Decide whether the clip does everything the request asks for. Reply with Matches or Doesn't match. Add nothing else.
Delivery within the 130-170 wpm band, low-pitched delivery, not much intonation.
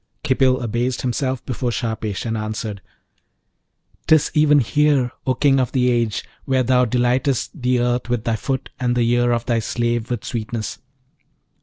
Matches